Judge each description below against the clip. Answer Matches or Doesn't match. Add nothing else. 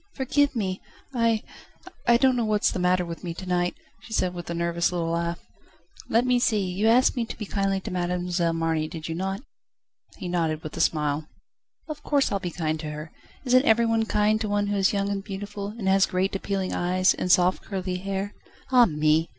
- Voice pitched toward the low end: Doesn't match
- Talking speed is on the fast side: Matches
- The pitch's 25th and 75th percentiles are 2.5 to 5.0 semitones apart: Matches